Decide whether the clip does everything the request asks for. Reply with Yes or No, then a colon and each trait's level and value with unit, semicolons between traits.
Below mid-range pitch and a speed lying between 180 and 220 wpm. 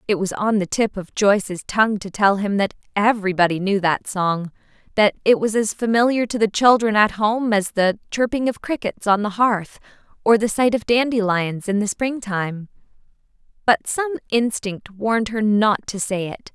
No: high, 210 Hz; average, 190 wpm